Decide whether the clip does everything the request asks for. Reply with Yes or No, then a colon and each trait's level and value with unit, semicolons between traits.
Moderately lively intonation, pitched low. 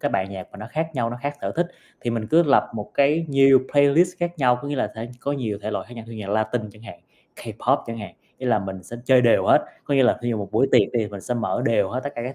Yes: average, 4.6 semitones; low, 120 Hz